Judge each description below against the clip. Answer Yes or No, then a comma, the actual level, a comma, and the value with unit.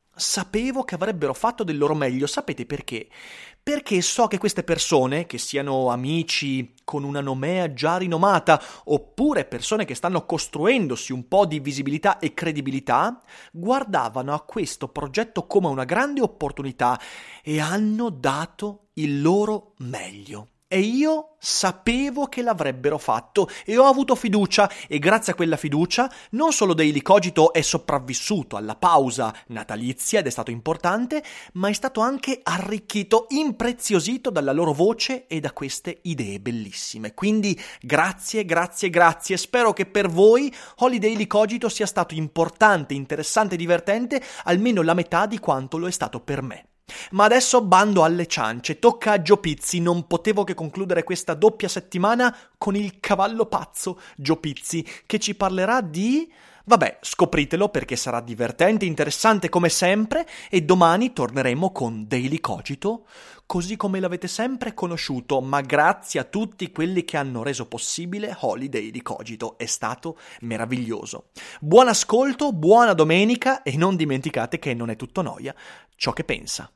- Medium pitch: Yes, medium, 175 Hz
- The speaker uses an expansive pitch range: Yes, wide, 6.6 semitones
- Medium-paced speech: Yes, average, 145 wpm